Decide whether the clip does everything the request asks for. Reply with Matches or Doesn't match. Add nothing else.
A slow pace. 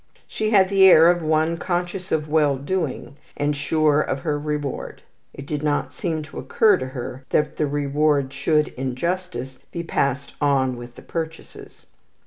Doesn't match